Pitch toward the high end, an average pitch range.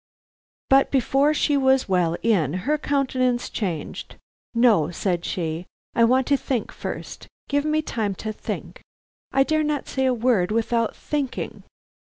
No: high, 245 Hz; wide, 5.9 semitones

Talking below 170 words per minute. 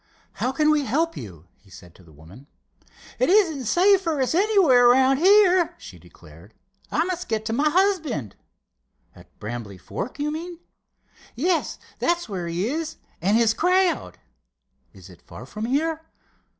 Yes: average, 160 wpm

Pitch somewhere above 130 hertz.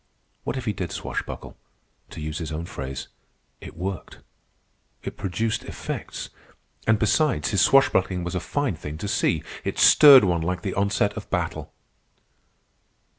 No: very low, 95 Hz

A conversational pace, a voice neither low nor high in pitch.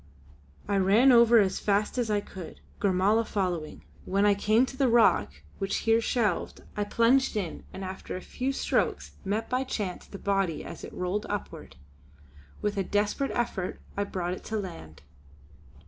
No: average, 170 wpm; high, 205 Hz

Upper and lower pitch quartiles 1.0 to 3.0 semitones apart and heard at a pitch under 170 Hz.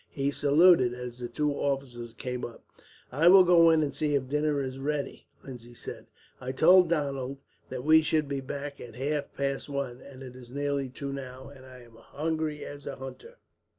Yes: narrow, 2.6 semitones; medium, 140 Hz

